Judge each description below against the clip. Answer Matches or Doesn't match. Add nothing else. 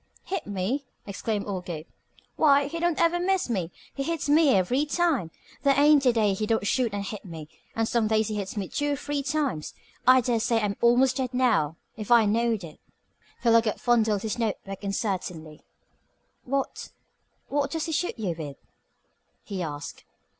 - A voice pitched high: Matches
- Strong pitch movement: Matches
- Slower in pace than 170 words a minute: Doesn't match